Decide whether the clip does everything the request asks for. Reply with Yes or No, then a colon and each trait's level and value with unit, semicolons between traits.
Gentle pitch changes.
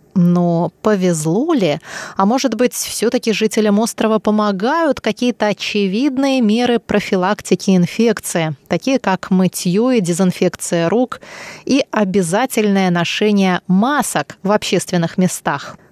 No: average, 4.0 semitones